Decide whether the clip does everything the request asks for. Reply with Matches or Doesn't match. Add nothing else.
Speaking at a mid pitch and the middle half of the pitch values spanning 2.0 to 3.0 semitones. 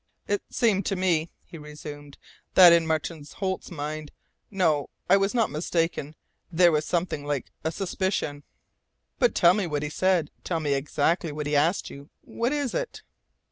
Doesn't match